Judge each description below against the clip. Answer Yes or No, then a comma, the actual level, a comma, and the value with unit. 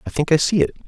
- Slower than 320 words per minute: No, fast, 345 wpm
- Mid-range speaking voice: Yes, medium, 155 Hz